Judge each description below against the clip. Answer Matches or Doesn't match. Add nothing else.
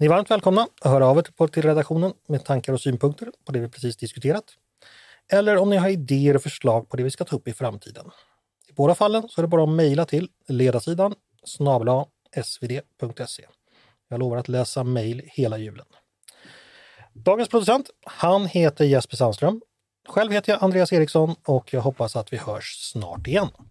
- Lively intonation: Matches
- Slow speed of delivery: Doesn't match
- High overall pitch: Doesn't match